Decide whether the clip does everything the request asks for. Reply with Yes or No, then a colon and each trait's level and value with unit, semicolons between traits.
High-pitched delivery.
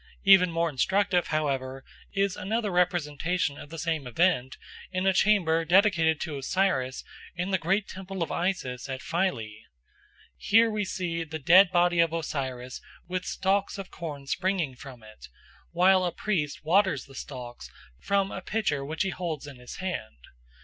No: medium, 170 Hz